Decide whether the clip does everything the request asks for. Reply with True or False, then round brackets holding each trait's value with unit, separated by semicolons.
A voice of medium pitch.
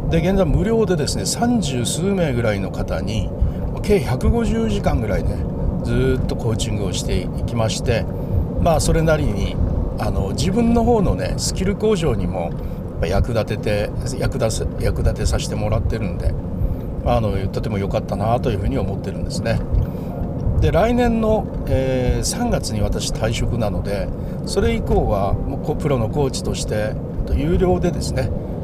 False (115 Hz)